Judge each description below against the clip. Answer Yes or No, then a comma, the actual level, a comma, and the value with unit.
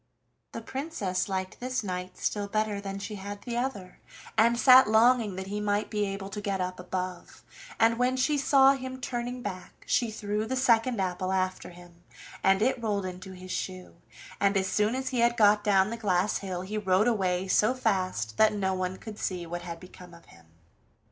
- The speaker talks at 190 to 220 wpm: Yes, average, 200 wpm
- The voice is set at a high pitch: Yes, high, 205 Hz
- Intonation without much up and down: No, average, 3.8 semitones